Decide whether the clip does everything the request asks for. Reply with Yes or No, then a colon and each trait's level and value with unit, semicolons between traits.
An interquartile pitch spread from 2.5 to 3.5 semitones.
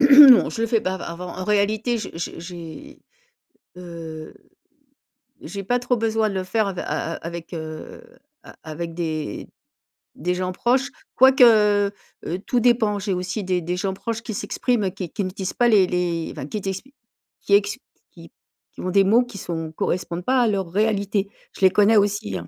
No: average, 3.9 semitones